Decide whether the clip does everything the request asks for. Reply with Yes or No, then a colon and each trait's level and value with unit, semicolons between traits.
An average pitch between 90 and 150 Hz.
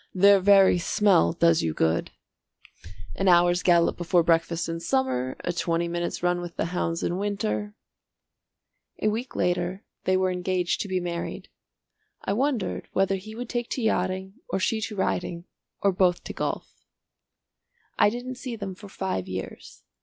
No: medium, 185 Hz